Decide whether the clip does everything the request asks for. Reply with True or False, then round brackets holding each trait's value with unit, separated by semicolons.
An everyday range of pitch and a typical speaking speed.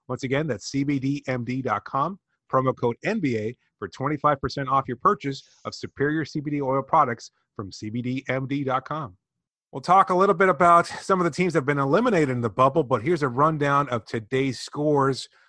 True (3.2 semitones; 165 wpm)